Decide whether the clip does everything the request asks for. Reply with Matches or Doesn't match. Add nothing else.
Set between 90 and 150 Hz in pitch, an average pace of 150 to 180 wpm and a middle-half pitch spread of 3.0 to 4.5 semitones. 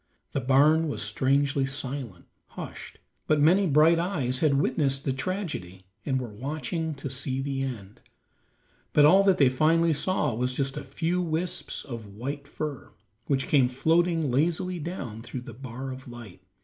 Matches